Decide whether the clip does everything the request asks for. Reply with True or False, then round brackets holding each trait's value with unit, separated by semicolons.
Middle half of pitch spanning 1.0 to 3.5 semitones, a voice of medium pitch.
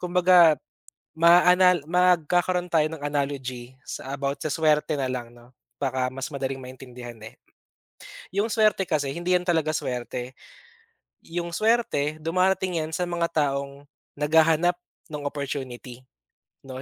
False (4.7 semitones; 150 Hz)